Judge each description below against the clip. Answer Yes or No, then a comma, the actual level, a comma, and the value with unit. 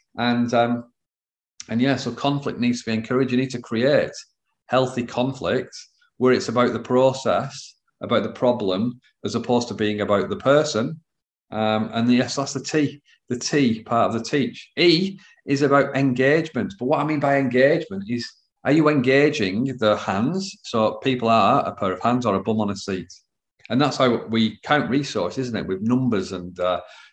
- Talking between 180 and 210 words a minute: Yes, average, 190 wpm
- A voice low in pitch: Yes, low, 125 Hz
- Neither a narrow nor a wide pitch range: Yes, average, 3.9 semitones